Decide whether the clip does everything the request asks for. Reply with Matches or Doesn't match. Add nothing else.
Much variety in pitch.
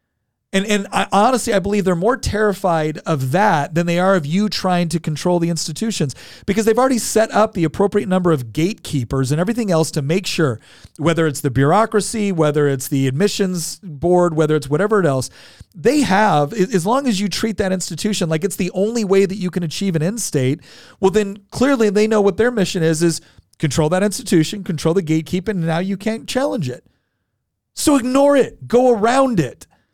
Doesn't match